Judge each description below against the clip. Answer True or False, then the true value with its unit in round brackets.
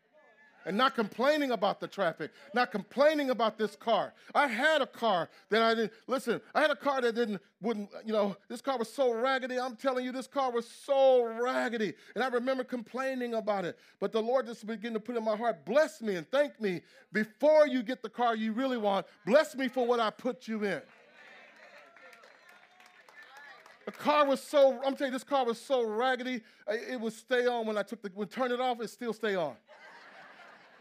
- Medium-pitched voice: False (245 Hz)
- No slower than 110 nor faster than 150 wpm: False (205 wpm)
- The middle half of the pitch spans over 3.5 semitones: False (3.2 semitones)